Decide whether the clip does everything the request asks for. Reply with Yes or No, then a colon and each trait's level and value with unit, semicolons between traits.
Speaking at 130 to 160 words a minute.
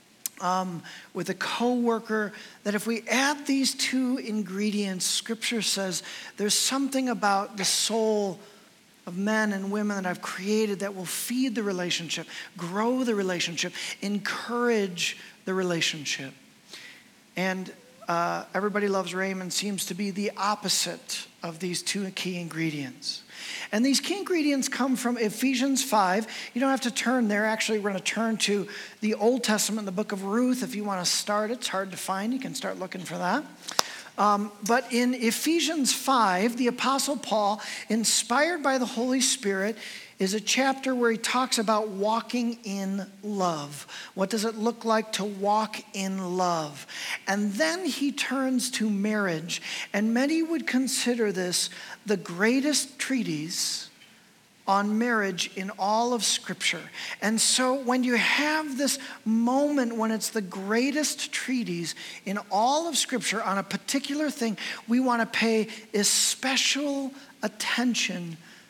Yes: average, 150 wpm